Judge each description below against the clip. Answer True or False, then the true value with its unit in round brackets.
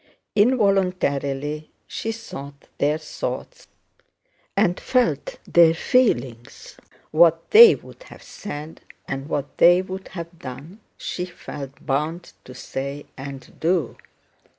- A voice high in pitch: False (160 Hz)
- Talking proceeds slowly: True (110 wpm)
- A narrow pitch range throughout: False (5.0 semitones)